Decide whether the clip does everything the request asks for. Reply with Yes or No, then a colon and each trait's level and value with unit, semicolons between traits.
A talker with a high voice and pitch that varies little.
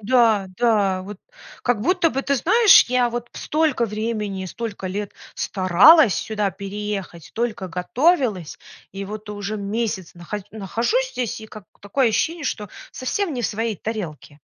No: high, 215 Hz; average, 3.9 semitones